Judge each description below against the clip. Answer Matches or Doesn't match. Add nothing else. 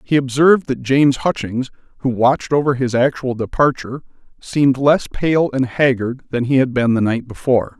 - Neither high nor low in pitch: Doesn't match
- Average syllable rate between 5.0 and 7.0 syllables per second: Matches